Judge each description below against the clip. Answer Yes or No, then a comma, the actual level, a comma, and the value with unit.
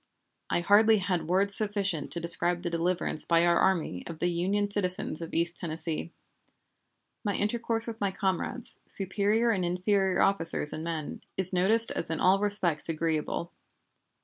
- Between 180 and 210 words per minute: No, average, 155 wpm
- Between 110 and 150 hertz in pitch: No, medium, 185 Hz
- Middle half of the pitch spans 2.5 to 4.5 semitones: Yes, average, 3.3 semitones